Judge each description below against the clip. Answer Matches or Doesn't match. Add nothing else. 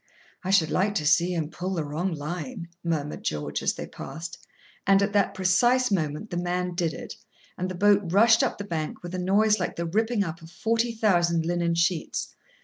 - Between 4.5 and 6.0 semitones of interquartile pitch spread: Doesn't match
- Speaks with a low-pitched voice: Doesn't match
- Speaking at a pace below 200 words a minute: Doesn't match